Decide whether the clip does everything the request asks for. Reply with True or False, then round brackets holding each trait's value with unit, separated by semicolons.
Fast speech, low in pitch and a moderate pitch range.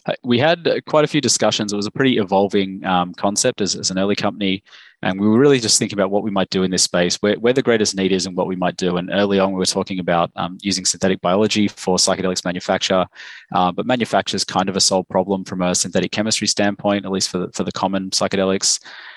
False (245 wpm; 95 Hz; 1.9 semitones)